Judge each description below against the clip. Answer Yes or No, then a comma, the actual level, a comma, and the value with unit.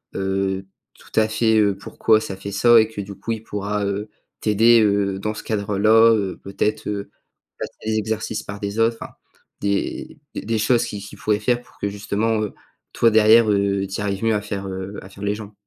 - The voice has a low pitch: Yes, low, 105 Hz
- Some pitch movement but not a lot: No, narrow, 1.8 semitones